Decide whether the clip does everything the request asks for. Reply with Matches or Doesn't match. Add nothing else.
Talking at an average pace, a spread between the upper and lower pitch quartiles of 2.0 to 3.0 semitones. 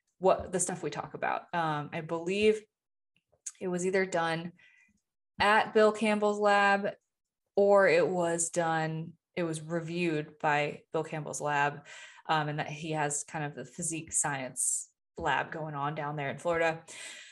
Doesn't match